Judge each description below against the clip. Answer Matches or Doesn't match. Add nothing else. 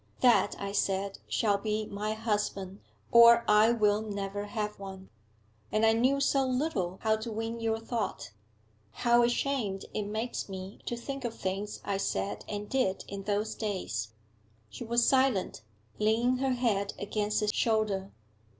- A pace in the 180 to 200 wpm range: Doesn't match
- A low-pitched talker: Doesn't match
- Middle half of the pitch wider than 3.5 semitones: Doesn't match